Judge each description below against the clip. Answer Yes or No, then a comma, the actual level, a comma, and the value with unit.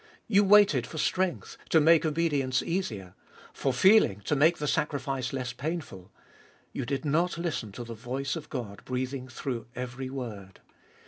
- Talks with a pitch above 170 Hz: No, low, 135 Hz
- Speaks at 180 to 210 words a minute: No, average, 155 wpm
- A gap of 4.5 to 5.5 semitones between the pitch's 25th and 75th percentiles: Yes, average, 4.8 semitones